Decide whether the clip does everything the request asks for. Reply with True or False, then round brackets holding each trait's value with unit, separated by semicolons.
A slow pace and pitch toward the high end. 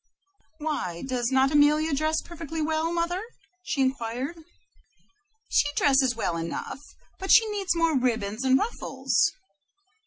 True (125 wpm; 285 Hz)